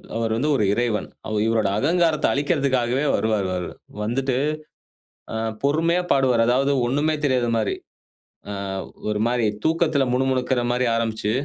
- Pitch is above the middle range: No, low, 125 Hz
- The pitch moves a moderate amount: Yes, average, 3.9 semitones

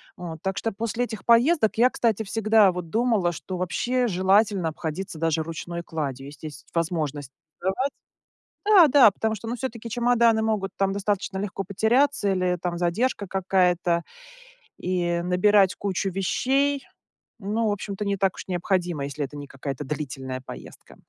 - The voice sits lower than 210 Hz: Yes, high, 190 Hz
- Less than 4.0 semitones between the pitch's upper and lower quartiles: No, average, 4.4 semitones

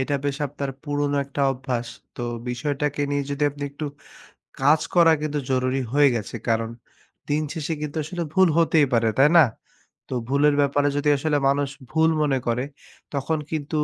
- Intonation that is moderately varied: No, narrow, 1.9 semitones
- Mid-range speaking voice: Yes, medium, 145 Hz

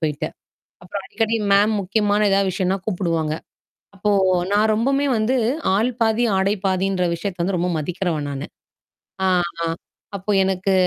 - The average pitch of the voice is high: Yes, high, 195 Hz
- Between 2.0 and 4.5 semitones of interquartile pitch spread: Yes, average, 2.8 semitones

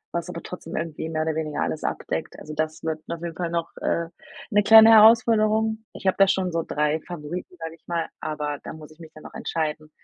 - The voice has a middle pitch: Yes, medium, 165 Hz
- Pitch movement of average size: Yes, average, 3.0 semitones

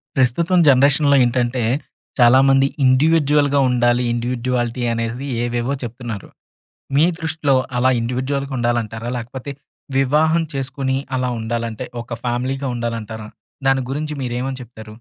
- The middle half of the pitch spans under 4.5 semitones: Yes, narrow, 2.4 semitones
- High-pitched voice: No, low, 125 Hz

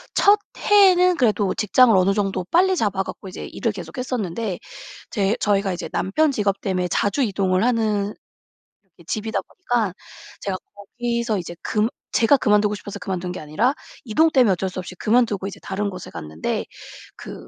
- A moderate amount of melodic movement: Yes, average, 4.1 semitones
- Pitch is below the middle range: No, high, 205 Hz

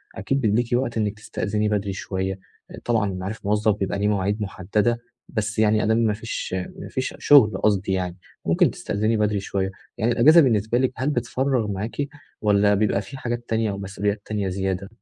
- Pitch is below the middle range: Yes, low, 105 Hz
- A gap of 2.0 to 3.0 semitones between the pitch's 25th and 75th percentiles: Yes, average, 2.7 semitones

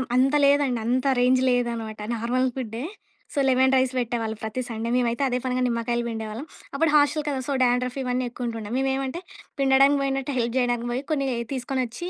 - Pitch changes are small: Yes, narrow, 2.3 semitones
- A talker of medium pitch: No, very high, 250 Hz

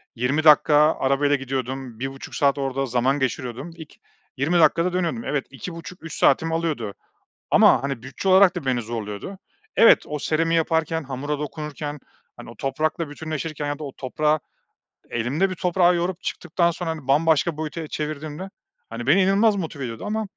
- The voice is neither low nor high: Yes, medium, 150 Hz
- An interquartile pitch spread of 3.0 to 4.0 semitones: Yes, average, 3.7 semitones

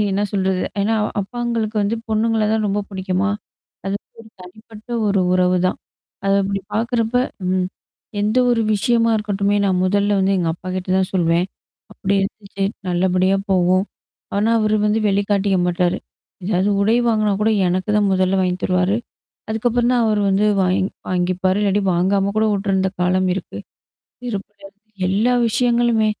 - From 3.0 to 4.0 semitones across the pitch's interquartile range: No, narrow, 2.6 semitones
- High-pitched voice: Yes, high, 200 Hz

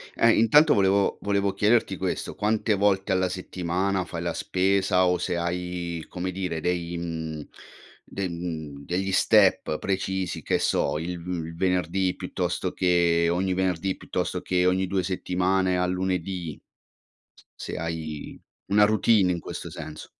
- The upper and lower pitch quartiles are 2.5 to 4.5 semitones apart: No, narrow, 2.0 semitones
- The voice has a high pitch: No, very low, 90 Hz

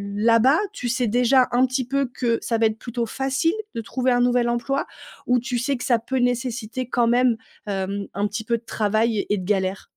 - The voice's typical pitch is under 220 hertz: No, high, 240 Hz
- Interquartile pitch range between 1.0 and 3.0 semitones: Yes, narrow, 2.4 semitones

